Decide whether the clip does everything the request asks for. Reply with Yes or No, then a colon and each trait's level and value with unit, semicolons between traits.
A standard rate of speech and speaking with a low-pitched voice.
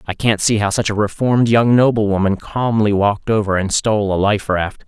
No: fast, 210 wpm; low, 105 Hz